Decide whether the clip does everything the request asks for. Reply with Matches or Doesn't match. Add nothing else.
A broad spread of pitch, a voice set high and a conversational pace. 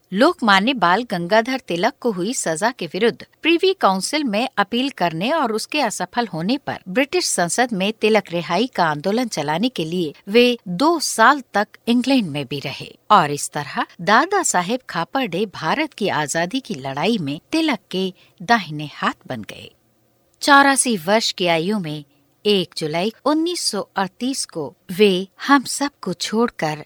Matches